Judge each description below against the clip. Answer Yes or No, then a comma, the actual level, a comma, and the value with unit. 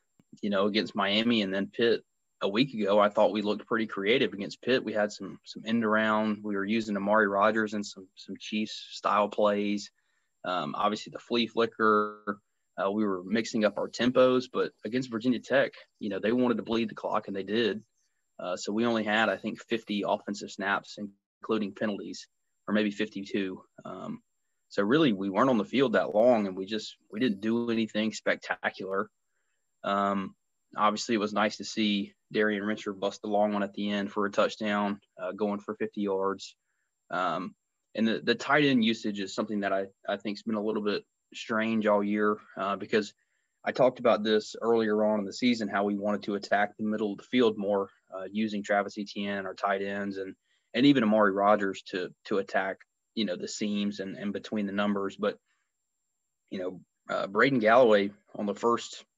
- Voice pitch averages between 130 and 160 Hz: No, low, 105 Hz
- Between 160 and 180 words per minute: No, average, 200 wpm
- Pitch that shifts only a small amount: Yes, narrow, 1.5 semitones